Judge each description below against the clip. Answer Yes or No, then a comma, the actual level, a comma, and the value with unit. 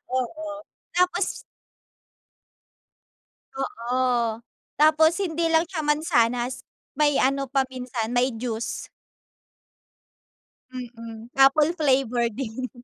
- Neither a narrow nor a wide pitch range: Yes, average, 4.2 semitones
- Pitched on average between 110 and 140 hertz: No, very high, 260 Hz